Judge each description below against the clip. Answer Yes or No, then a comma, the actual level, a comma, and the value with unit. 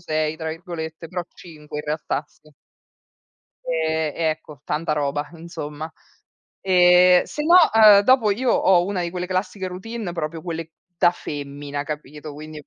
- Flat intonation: No, average, 3.1 semitones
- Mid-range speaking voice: Yes, medium, 165 Hz